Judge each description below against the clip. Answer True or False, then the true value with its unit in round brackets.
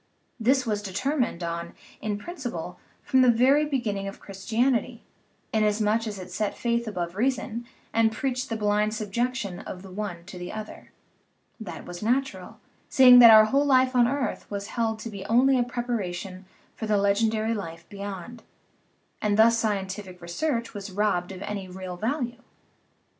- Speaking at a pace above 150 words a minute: True (165 wpm)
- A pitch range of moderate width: True (3.8 semitones)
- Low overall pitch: False (215 Hz)